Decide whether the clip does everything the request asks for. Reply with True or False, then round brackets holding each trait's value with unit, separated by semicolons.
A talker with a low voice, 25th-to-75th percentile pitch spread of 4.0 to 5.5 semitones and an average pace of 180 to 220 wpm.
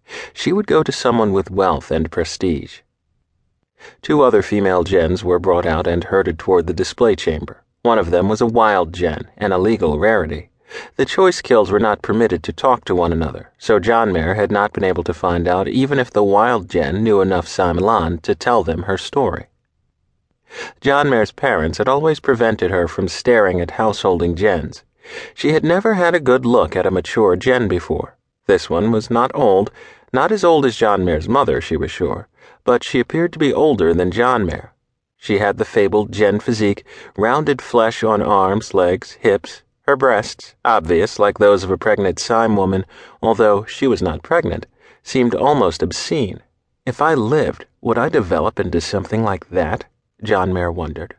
True (100 Hz; 4.6 semitones; 185 wpm)